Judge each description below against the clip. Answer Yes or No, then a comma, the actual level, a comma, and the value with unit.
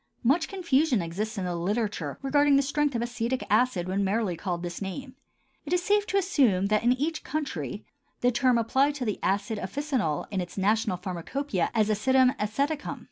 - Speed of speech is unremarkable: Yes, average, 190 wpm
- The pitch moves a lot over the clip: Yes, wide, 6.3 semitones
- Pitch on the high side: Yes, high, 235 Hz